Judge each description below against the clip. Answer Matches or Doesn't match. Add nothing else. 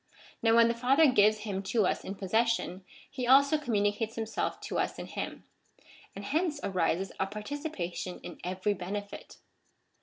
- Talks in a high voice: Matches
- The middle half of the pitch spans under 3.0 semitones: Doesn't match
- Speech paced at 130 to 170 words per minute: Matches